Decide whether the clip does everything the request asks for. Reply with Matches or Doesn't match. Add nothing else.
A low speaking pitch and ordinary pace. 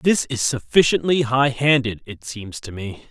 Matches